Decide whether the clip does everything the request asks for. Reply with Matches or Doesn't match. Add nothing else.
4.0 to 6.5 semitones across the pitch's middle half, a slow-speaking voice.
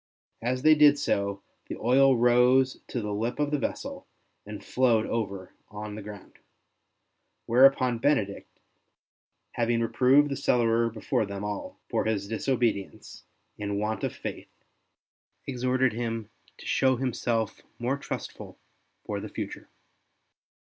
Doesn't match